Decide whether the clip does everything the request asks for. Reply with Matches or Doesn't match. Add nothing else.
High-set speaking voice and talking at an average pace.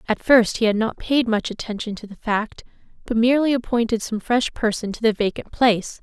Doesn't match